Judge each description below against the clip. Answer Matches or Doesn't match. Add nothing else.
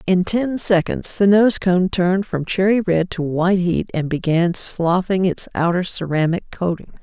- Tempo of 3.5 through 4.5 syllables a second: Matches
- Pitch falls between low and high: Matches